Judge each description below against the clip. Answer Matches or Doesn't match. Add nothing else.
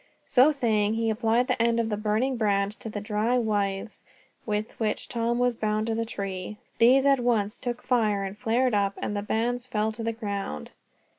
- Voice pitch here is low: Doesn't match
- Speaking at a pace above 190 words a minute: Matches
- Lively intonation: Doesn't match